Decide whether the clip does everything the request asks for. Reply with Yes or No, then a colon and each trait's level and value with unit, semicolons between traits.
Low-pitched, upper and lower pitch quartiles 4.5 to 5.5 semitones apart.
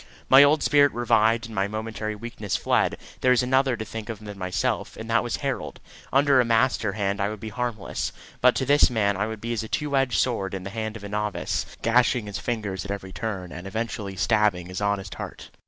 No: low, 110 Hz; average, 3.2 semitones